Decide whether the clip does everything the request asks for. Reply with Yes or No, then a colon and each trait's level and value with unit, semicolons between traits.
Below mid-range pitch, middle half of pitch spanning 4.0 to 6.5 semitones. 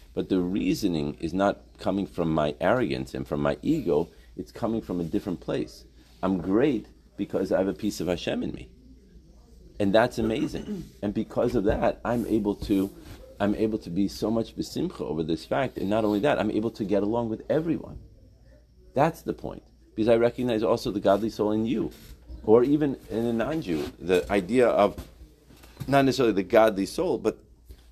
Yes: low, 100 Hz; wide, 5.4 semitones